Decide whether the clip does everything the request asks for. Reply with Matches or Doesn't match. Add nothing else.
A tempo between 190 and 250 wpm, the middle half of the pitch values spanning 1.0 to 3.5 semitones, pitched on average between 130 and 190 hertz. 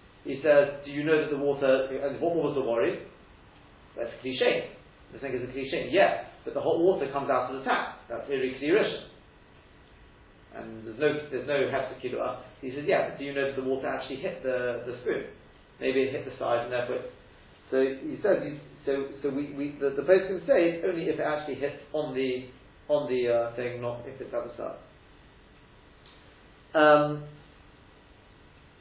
Matches